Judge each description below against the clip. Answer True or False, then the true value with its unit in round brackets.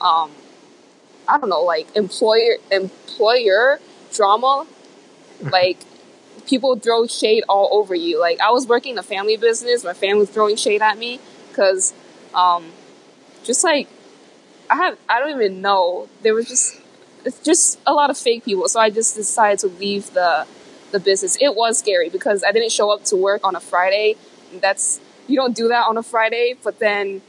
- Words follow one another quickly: False (180 wpm)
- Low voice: False (215 Hz)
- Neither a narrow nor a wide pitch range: True (4.2 semitones)